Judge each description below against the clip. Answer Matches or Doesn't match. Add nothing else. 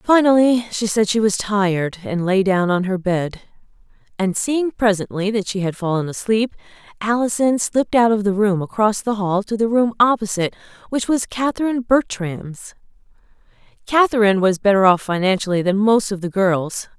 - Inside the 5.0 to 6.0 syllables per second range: Matches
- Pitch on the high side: Matches